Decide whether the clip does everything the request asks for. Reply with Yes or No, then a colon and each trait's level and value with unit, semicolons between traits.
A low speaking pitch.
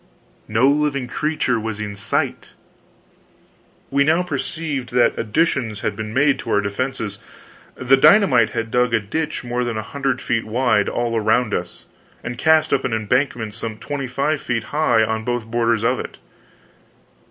Yes: low, 120 Hz